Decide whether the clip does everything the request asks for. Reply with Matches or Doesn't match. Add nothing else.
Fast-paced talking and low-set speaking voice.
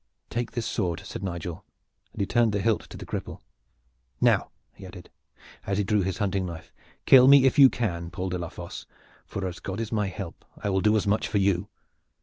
Matches